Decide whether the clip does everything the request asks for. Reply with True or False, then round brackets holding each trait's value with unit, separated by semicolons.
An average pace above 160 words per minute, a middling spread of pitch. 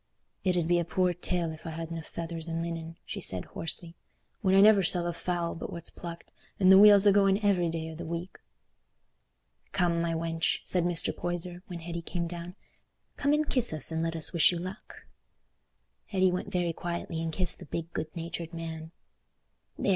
False (200 wpm; 1.7 semitones)